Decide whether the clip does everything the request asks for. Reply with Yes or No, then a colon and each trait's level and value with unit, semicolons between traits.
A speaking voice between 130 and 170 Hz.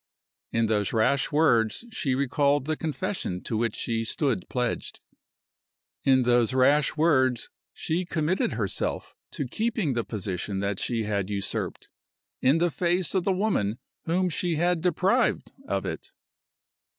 Yes: low, 135 Hz